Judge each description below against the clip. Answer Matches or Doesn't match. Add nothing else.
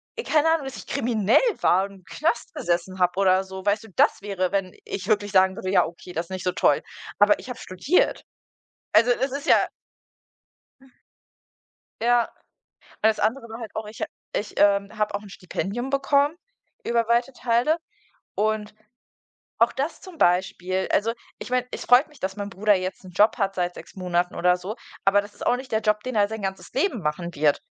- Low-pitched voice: Doesn't match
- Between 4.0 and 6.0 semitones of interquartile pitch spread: Matches